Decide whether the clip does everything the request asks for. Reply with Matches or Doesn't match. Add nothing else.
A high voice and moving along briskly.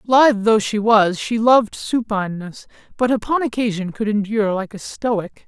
Doesn't match